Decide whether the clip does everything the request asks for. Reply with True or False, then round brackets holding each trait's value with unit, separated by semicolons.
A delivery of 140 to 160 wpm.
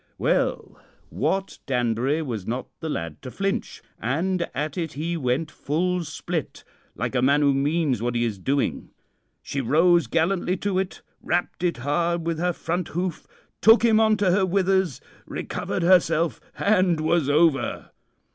True (155 wpm)